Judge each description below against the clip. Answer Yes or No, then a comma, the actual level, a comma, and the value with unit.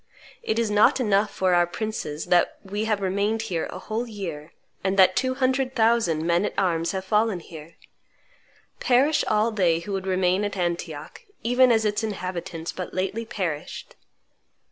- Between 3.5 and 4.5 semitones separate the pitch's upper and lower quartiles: Yes, average, 4.1 semitones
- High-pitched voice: Yes, high, 195 Hz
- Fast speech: No, average, 165 wpm